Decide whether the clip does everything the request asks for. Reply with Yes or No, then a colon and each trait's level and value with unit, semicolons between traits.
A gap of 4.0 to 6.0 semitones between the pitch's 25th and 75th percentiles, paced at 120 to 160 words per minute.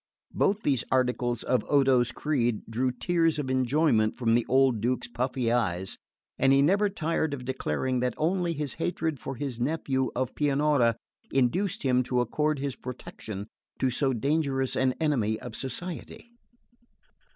No: average, 3.5 semitones; average, 155 wpm